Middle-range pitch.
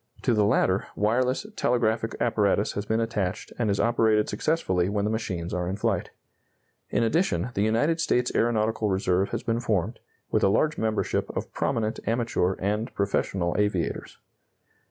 No: low, 110 Hz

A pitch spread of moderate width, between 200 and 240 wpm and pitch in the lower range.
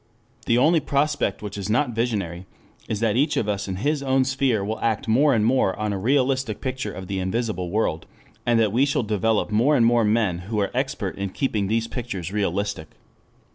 Yes: average, 4.4 semitones; fast, 205 wpm; low, 110 Hz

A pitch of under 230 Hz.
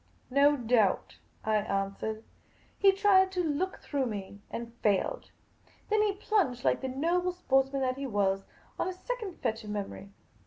No: very high, 270 Hz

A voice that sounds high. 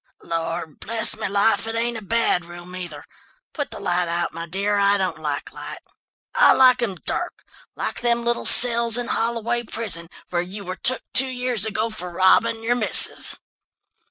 Yes: high, 210 Hz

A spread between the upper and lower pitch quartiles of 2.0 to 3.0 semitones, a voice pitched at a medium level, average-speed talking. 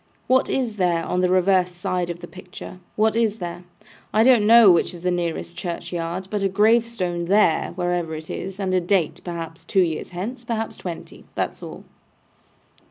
No: average, 3.4 semitones; medium, 180 Hz; average, 180 wpm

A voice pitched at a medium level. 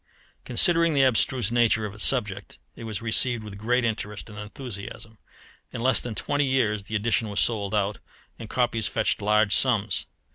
No: low, 110 Hz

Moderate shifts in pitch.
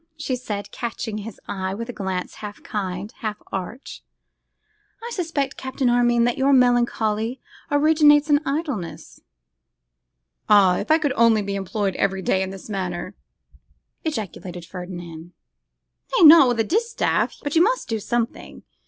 No: wide, 6.3 semitones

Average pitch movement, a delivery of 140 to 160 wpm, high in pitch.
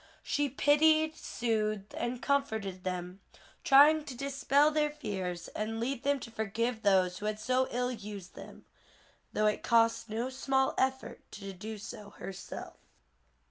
Yes: average, 4.9 semitones; average, 145 wpm; high, 230 Hz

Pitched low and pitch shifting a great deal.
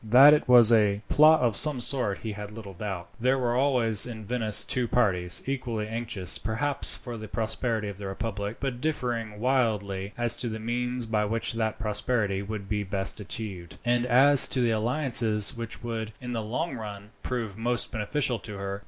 No: low, 115 Hz; average, 2.9 semitones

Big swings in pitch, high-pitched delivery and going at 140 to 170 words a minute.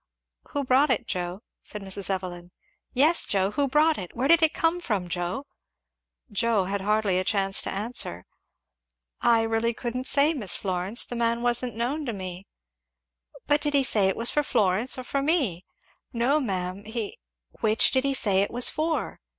No: wide, 5.8 semitones; high, 230 Hz; average, 180 wpm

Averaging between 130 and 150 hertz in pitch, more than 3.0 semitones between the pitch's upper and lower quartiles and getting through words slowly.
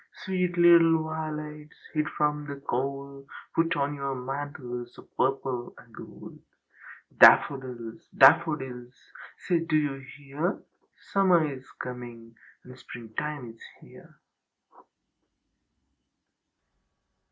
Yes: medium, 140 Hz; average, 3.5 semitones; slow, 95 wpm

